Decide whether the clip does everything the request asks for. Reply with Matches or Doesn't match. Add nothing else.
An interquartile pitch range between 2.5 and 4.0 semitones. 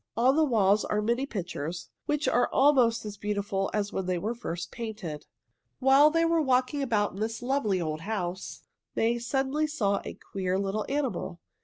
Doesn't match